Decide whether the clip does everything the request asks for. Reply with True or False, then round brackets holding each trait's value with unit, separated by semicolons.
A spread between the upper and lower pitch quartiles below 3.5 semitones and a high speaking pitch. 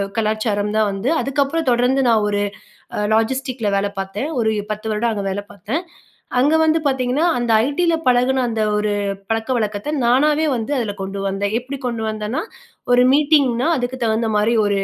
False (3.9 semitones; 235 Hz)